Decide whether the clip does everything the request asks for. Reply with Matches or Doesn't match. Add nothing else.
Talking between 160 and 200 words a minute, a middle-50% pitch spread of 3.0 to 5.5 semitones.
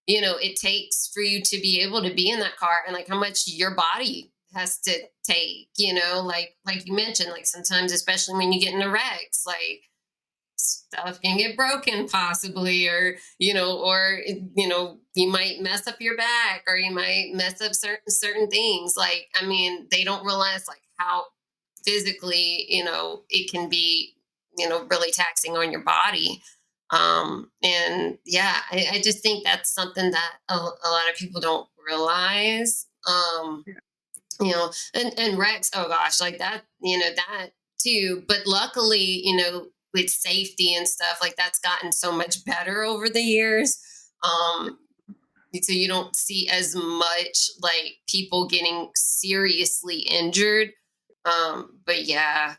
Doesn't match